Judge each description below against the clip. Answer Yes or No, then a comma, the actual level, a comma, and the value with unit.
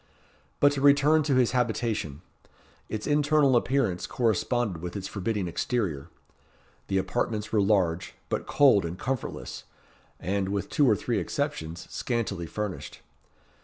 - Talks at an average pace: No, slow, 130 wpm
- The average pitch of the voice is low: Yes, low, 110 Hz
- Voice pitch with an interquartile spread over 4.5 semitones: Yes, wide, 5.6 semitones